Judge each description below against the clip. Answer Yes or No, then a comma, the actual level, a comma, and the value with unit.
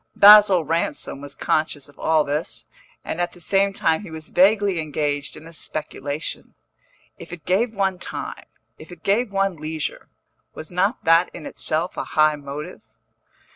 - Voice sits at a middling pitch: Yes, medium, 165 Hz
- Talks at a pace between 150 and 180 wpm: Yes, average, 165 wpm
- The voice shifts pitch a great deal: No, average, 4.0 semitones